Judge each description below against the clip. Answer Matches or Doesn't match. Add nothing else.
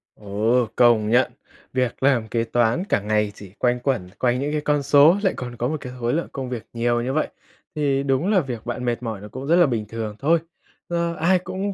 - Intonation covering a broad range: Doesn't match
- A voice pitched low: Matches